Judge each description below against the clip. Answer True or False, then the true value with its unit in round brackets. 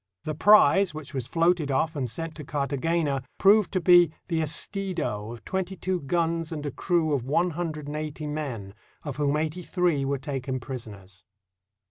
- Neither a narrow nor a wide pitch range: True (3.8 semitones)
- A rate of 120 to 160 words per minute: False (180 wpm)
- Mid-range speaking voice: True (155 Hz)